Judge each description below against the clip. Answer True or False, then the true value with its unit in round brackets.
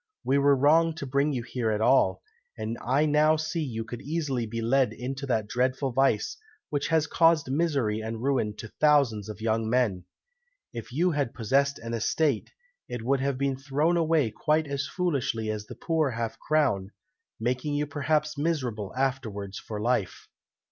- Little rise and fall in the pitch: False (4.7 semitones)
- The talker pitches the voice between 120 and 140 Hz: True (135 Hz)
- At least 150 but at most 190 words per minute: True (175 wpm)